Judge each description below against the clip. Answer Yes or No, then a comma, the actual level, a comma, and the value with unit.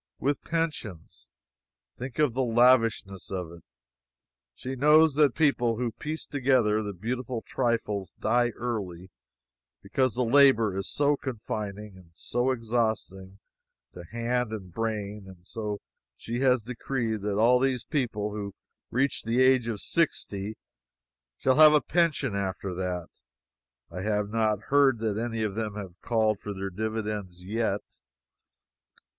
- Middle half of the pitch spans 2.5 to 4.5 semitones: Yes, average, 4.0 semitones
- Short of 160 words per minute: Yes, average, 140 wpm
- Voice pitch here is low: Yes, low, 115 Hz